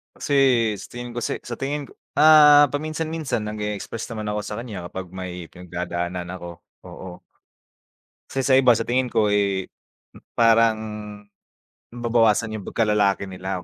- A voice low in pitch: Yes, low, 110 Hz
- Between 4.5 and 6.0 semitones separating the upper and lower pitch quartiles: Yes, average, 4.8 semitones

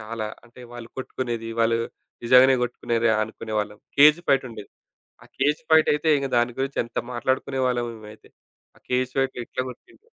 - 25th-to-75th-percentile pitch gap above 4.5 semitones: No, average, 2.7 semitones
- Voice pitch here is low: Yes, low, 125 Hz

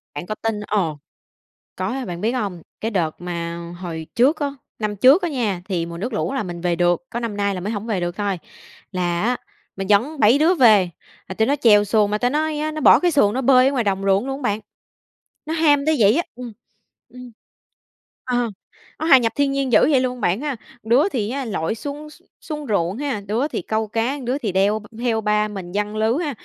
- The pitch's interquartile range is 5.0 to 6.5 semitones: Yes, average, 5.3 semitones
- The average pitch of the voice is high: Yes, high, 220 Hz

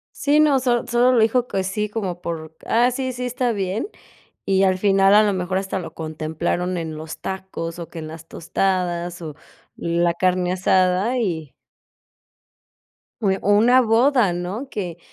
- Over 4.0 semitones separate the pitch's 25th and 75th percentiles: Yes, average, 4.7 semitones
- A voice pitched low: No, high, 190 Hz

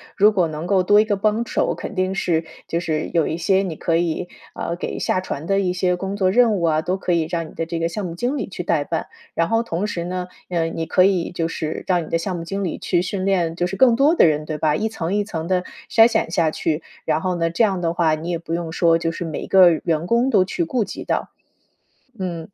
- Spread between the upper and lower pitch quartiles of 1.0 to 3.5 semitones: Yes, average, 2.9 semitones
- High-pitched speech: No, medium, 175 Hz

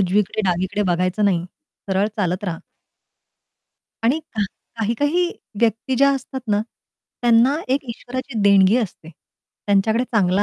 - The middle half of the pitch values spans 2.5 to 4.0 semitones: No, average, 4.4 semitones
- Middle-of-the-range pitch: No, high, 210 Hz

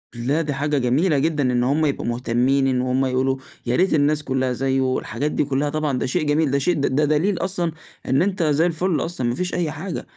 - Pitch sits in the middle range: Yes, medium, 145 Hz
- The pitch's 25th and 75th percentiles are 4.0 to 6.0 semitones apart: No, average, 3.2 semitones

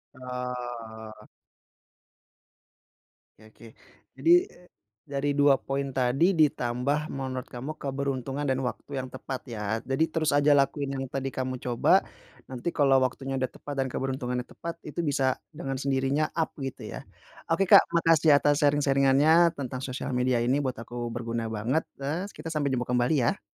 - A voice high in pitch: No, low, 135 Hz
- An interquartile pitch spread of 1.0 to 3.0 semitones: Yes, narrow, 2.5 semitones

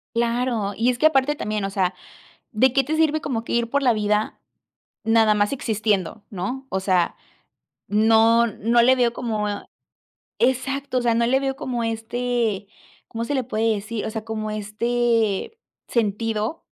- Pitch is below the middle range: No, high, 230 Hz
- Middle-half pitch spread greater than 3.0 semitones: No, average, 2.7 semitones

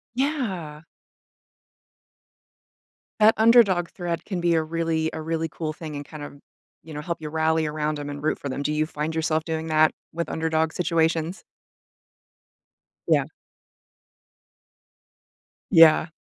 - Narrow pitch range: Yes, narrow, 1.6 semitones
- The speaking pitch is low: No, medium, 160 Hz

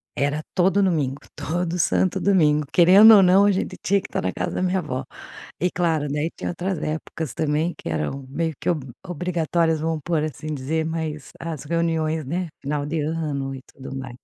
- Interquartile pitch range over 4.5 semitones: No, average, 3.1 semitones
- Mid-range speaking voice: Yes, medium, 160 Hz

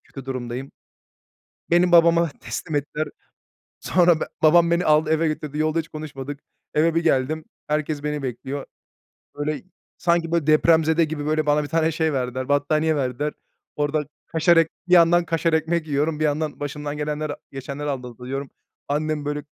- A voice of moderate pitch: Yes, medium, 155 Hz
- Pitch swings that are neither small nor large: No, narrow, 1.9 semitones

